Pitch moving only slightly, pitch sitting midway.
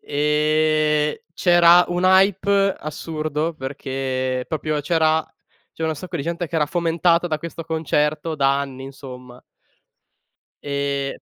No: average, 3.0 semitones; medium, 155 Hz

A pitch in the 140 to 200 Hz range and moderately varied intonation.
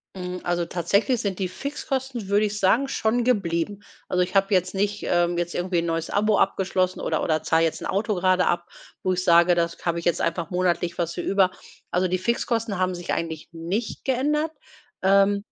Yes: medium, 185 Hz; average, 3.1 semitones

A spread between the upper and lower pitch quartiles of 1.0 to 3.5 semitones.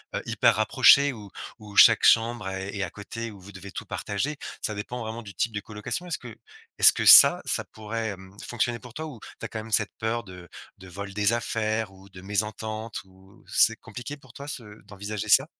Yes: average, 2.9 semitones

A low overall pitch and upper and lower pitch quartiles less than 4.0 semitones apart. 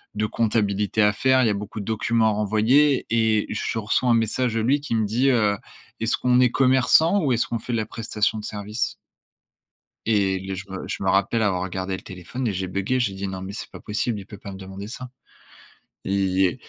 Yes: low, 110 Hz; average, 3.2 semitones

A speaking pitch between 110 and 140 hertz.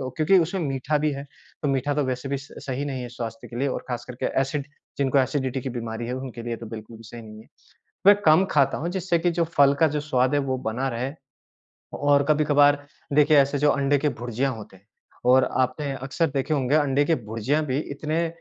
Yes: low, 135 Hz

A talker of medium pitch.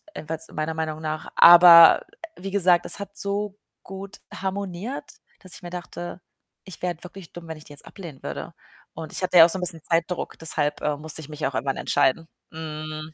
Yes: medium, 170 Hz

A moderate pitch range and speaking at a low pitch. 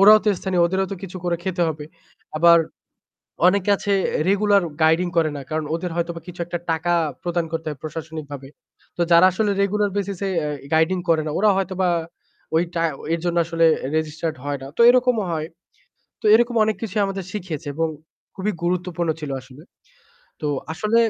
No: average, 3.5 semitones; medium, 175 Hz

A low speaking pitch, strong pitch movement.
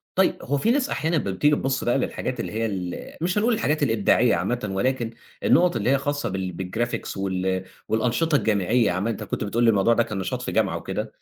Yes: low, 120 Hz; wide, 6.5 semitones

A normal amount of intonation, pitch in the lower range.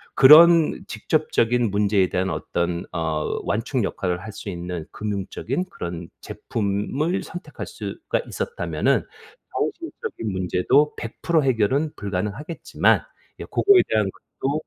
No: wide, 8.1 semitones; low, 110 Hz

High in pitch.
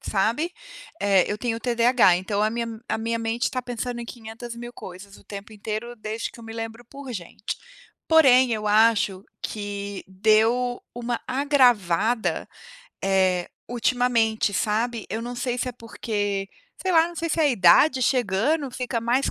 Yes: high, 230 Hz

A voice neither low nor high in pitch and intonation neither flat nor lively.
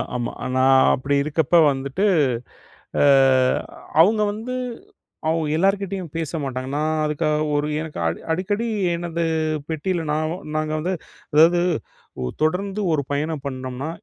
Yes: medium, 155 Hz; average, 3.9 semitones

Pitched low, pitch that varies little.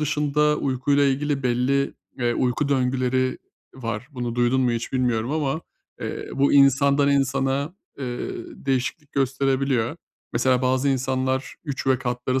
Yes: low, 130 Hz; narrow, 1.9 semitones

